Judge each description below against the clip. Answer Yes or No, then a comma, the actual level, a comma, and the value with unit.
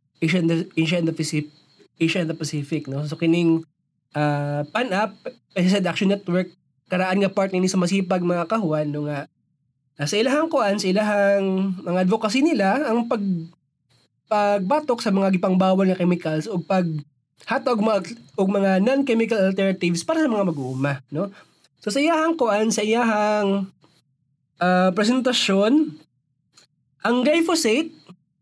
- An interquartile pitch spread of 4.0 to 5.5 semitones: Yes, average, 5.1 semitones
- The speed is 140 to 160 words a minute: Yes, average, 150 wpm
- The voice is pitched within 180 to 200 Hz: Yes, medium, 185 Hz